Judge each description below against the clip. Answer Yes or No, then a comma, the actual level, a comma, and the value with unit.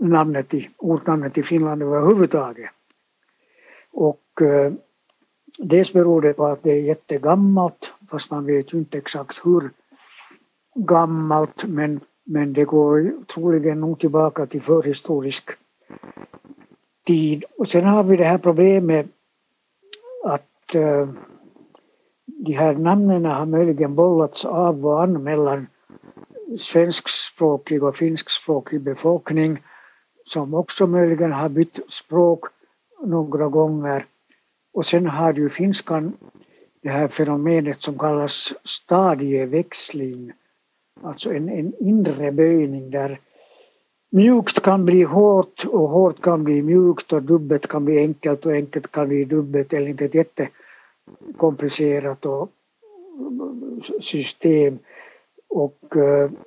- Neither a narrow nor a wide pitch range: Yes, average, 3.0 semitones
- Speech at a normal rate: No, slow, 115 wpm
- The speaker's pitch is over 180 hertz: No, medium, 160 Hz